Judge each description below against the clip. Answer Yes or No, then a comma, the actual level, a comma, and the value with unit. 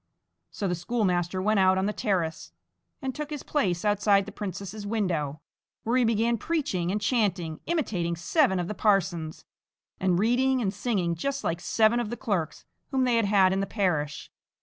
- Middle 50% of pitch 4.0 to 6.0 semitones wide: Yes, average, 4.6 semitones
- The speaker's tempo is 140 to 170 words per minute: No, average, 180 wpm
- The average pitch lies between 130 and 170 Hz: No, high, 200 Hz